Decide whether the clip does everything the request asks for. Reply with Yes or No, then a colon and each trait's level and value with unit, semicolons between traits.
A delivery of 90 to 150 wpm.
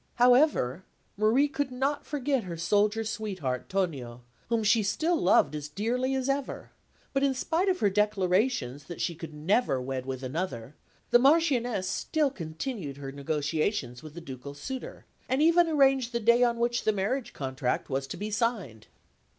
No: average, 165 wpm